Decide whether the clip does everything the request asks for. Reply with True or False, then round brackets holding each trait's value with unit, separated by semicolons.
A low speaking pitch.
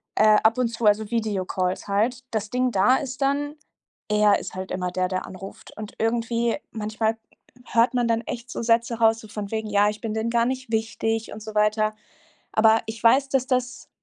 False (225 Hz)